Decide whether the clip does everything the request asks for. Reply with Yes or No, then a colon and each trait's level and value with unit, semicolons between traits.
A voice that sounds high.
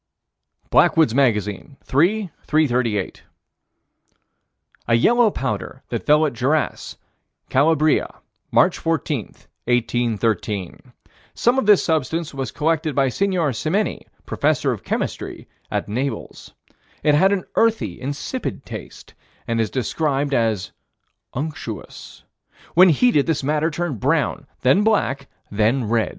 No: medium, 145 Hz